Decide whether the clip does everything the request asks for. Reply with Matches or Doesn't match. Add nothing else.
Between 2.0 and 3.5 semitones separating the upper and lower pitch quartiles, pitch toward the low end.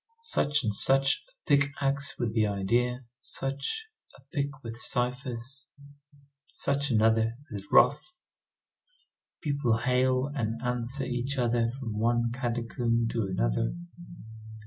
Matches